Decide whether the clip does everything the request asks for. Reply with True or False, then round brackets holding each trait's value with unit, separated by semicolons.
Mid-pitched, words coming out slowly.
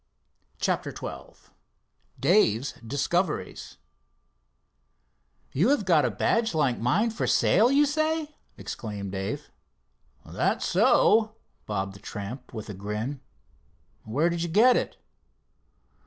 True (145 Hz; 110 wpm)